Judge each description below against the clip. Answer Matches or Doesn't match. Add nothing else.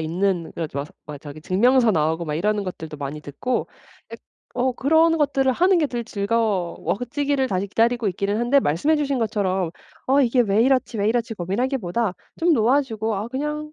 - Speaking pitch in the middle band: Doesn't match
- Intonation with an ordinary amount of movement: Doesn't match